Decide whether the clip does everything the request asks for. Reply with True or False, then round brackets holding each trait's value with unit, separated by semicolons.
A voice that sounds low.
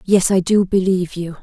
False (185 Hz)